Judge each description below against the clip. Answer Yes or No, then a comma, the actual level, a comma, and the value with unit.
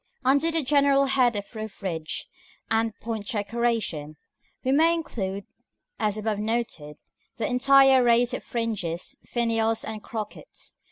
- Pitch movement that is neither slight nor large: Yes, average, 3.9 semitones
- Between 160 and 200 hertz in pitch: No, high, 230 Hz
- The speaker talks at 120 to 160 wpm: Yes, average, 145 wpm